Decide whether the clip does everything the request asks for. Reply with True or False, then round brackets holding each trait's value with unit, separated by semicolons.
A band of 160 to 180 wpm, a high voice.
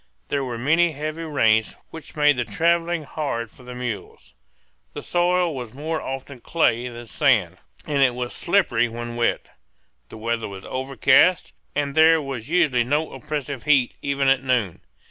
False (165 wpm; 135 Hz)